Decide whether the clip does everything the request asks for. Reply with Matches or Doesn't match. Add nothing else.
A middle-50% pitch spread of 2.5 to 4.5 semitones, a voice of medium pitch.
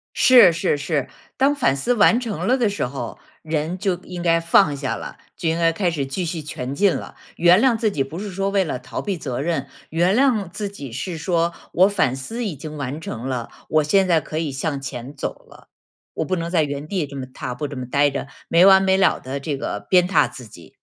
Doesn't match